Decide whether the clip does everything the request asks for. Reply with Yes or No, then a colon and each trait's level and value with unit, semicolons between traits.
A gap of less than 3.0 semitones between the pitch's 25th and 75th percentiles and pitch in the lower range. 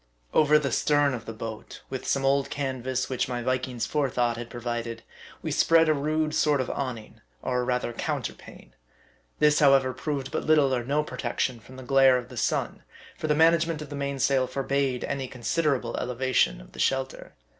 Yes: narrow, 2.6 semitones; low, 130 Hz